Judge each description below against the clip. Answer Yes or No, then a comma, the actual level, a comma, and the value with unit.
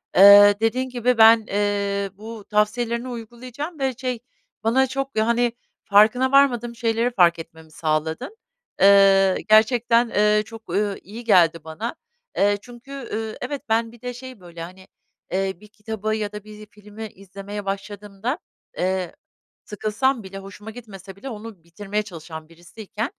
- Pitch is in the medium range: No, high, 215 Hz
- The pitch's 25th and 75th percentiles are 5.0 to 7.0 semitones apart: No, average, 3.3 semitones